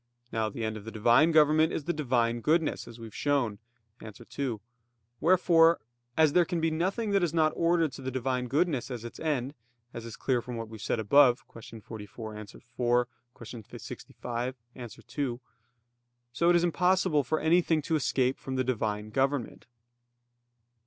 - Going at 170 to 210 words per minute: Yes, average, 180 wpm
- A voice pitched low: Yes, low, 130 Hz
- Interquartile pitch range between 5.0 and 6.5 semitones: Yes, wide, 5.4 semitones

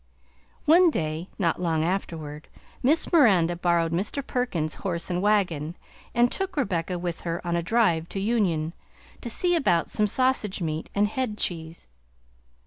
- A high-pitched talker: No, medium, 180 Hz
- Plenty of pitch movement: Yes, wide, 5.9 semitones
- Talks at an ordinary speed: Yes, average, 150 wpm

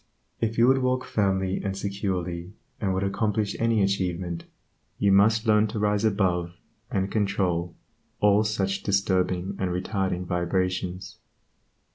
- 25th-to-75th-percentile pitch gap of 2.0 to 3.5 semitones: Yes, narrow, 2.4 semitones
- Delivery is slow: Yes, slow, 130 wpm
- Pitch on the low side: Yes, very low, 95 Hz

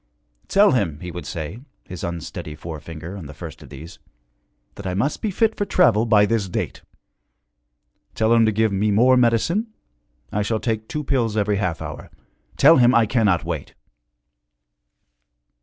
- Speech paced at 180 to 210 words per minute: No, average, 165 wpm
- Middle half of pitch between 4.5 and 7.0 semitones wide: Yes, average, 5.2 semitones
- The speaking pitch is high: No, low, 105 Hz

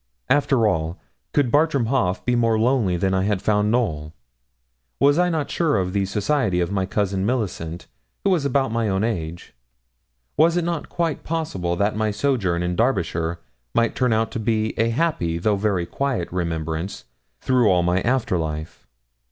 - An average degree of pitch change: No, wide, 6.7 semitones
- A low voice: Yes, low, 105 Hz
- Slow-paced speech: No, average, 170 wpm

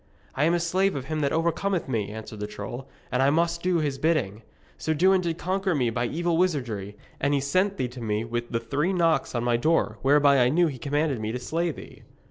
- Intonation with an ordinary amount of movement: No, wide, 5.8 semitones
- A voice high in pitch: No, medium, 145 Hz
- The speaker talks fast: Yes, fast, 235 wpm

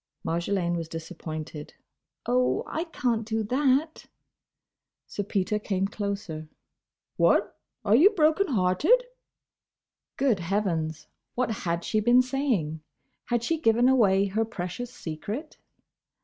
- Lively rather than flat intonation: Yes, wide, 6.6 semitones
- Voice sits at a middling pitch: No, high, 210 Hz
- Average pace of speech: No, slow, 110 wpm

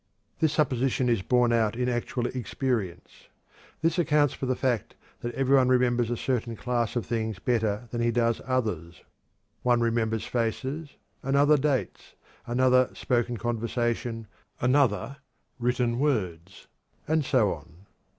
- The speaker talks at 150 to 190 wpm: No, slow, 135 wpm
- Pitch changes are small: Yes, narrow, 2.3 semitones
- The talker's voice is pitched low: Yes, low, 120 Hz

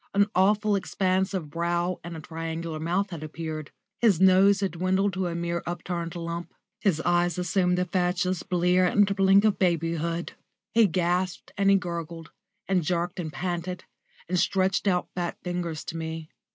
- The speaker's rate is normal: Yes, average, 165 wpm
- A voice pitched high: No, medium, 180 Hz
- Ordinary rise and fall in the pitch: No, narrow, 2.0 semitones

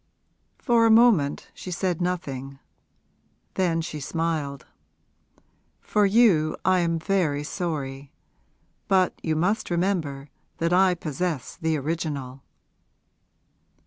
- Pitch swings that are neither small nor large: Yes, average, 4.2 semitones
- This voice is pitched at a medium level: Yes, medium, 165 Hz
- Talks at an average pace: No, slow, 105 wpm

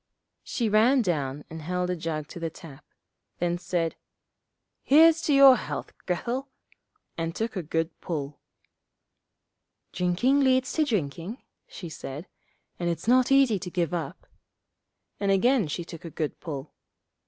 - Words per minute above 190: No, average, 150 wpm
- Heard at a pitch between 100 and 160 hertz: No, medium, 180 Hz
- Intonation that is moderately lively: No, wide, 7.0 semitones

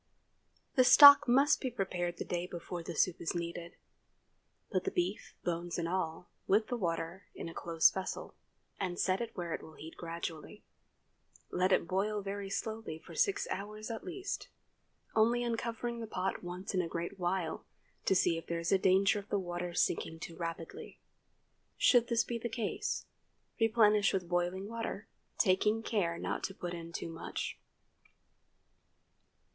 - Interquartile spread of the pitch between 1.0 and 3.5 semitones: No, average, 4.2 semitones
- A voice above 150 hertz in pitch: Yes, medium, 185 Hz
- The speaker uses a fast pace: No, average, 165 wpm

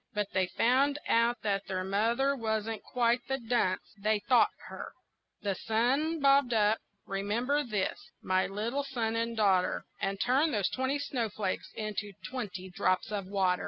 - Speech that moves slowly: No, average, 155 wpm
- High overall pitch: Yes, high, 220 Hz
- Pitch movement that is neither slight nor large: Yes, average, 4.2 semitones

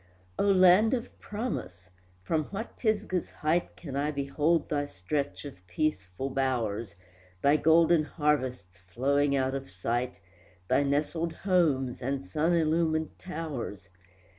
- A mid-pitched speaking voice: Yes, medium, 145 Hz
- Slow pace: Yes, slow, 125 wpm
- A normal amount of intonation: Yes, average, 4.7 semitones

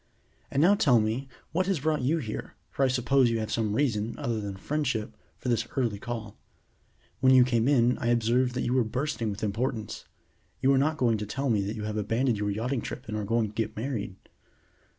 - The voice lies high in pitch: No, low, 120 Hz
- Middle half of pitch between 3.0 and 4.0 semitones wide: Yes, average, 3.5 semitones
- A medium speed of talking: No, fast, 220 wpm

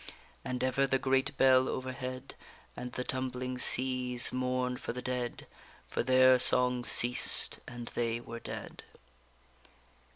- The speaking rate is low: Yes, slow, 130 wpm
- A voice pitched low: Yes, low, 125 Hz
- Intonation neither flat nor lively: No, narrow, 0.6 semitones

